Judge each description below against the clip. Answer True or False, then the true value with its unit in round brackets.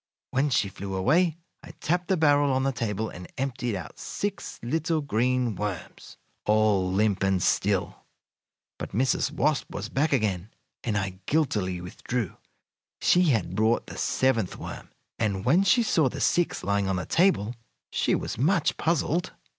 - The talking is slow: False (160 wpm)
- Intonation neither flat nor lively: False (7.3 semitones)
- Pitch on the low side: True (120 Hz)